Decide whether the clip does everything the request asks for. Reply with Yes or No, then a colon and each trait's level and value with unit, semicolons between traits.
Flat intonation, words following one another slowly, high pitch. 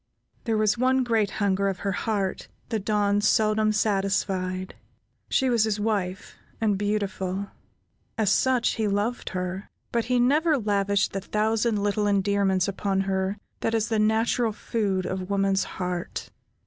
No: narrow, 2.3 semitones; average, 150 wpm; high, 205 Hz